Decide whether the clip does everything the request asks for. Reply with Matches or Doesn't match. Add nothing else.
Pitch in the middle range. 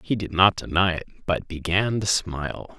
Doesn't match